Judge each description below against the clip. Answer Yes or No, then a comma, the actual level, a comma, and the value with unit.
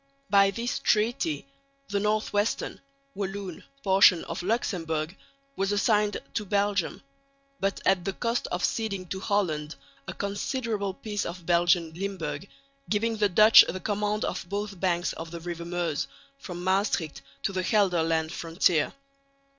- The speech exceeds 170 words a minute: No, average, 140 wpm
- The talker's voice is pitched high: Yes, high, 195 Hz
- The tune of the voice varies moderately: Yes, average, 3.1 semitones